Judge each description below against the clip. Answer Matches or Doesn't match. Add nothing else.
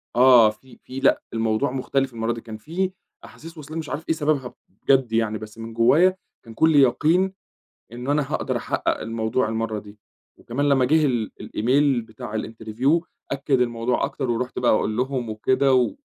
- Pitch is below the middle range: Matches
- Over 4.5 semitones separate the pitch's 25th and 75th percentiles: Doesn't match